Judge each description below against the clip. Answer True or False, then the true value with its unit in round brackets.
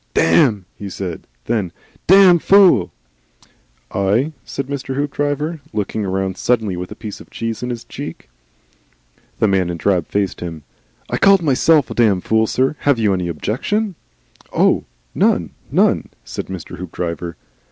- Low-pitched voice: True (110 Hz)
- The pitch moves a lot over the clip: True (7.3 semitones)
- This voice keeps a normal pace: True (150 wpm)